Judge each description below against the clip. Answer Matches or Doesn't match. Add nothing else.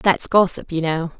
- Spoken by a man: Doesn't match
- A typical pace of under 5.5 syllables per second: Matches